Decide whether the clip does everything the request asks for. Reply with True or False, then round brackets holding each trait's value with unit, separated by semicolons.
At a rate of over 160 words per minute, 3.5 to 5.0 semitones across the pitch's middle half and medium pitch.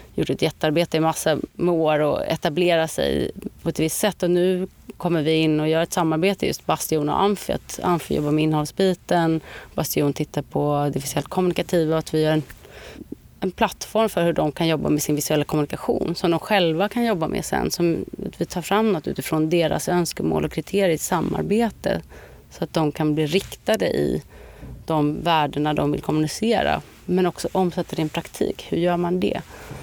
False (195 wpm; 2.8 semitones; 165 Hz)